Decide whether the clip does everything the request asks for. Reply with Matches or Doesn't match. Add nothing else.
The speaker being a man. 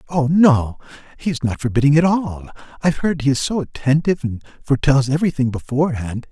Matches